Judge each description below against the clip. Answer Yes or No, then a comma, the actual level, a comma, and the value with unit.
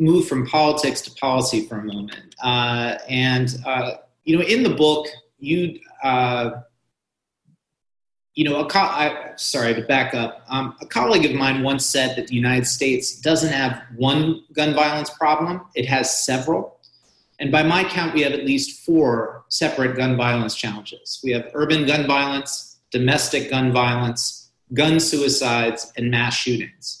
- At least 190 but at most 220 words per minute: No, average, 160 wpm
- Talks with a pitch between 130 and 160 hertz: Yes, low, 135 Hz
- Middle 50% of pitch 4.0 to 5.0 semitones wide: No, average, 3.6 semitones